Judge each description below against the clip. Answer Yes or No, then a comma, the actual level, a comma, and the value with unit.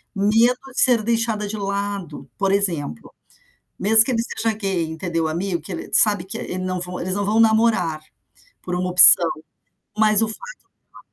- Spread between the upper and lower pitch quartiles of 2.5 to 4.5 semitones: Yes, average, 3.6 semitones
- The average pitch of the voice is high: Yes, high, 200 Hz